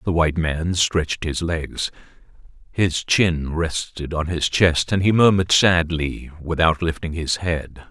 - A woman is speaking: No, male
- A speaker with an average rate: Yes, average, 150 wpm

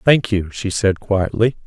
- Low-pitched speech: Yes, low, 105 Hz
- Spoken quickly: No, average, 180 wpm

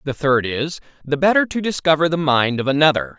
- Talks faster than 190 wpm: Yes, fast, 205 wpm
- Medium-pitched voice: Yes, medium, 150 Hz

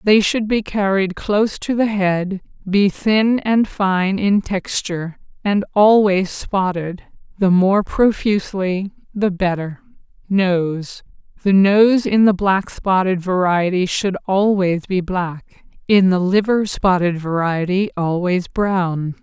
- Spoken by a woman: Yes, female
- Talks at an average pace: No, slow, 120 wpm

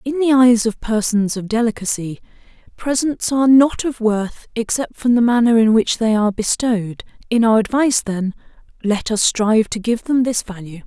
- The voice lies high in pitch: Yes, high, 230 Hz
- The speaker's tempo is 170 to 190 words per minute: Yes, average, 180 wpm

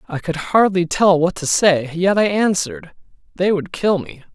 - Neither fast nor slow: Yes, average, 195 wpm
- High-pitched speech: No, medium, 175 Hz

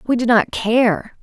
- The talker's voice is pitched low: No, high, 225 Hz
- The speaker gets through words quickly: No, average, 195 wpm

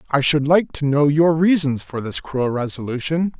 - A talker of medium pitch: Yes, medium, 150 Hz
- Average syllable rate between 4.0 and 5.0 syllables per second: Yes, 4.7 syllables/s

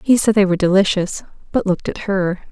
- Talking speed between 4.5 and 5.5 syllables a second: No, 6.4 syllables/s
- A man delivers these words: No, female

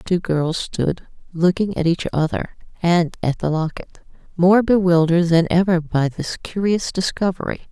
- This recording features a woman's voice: Yes, female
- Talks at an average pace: Yes, average, 155 wpm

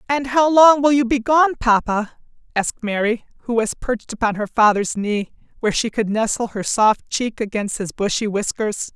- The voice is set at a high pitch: Yes, high, 230 Hz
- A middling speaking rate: Yes, average, 190 wpm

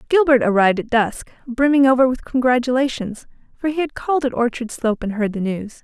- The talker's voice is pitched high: Yes, very high, 250 Hz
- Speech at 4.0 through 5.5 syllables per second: No, 5.9 syllables/s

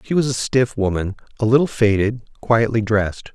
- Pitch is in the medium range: No, low, 115 Hz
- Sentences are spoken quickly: No, average, 180 wpm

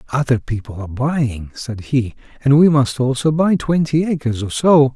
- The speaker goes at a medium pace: Yes, average, 180 wpm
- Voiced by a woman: No, male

